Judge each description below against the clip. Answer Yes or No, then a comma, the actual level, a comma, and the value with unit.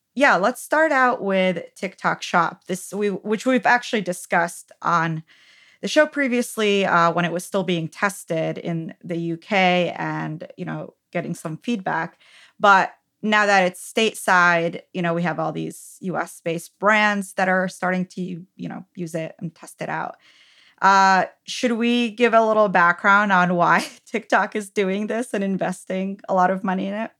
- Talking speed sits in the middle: Yes, average, 175 wpm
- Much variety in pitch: No, average, 3.6 semitones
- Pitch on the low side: No, medium, 185 Hz